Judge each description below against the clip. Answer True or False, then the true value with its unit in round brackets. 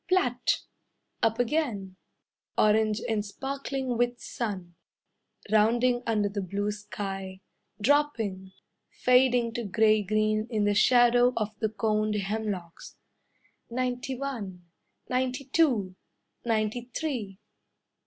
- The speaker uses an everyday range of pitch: True (3.3 semitones)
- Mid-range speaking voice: False (220 Hz)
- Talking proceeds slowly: True (105 wpm)